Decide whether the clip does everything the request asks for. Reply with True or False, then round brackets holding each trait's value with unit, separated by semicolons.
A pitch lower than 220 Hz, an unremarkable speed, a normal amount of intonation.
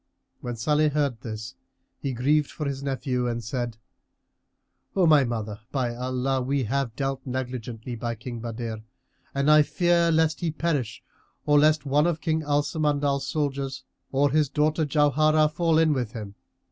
True (140 Hz; 160 wpm; 3.7 semitones)